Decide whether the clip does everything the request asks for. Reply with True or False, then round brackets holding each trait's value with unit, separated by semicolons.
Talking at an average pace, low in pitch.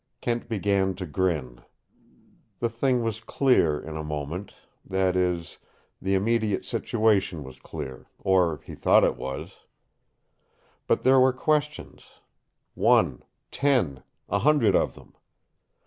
False (125 wpm; 95 Hz)